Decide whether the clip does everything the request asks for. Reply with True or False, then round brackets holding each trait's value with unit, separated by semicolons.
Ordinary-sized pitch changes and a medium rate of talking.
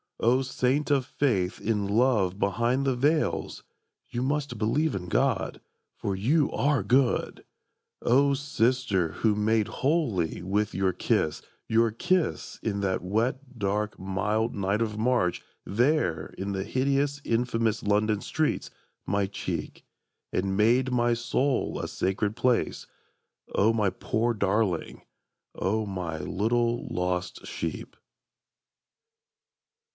False (4.5 semitones; 120 wpm)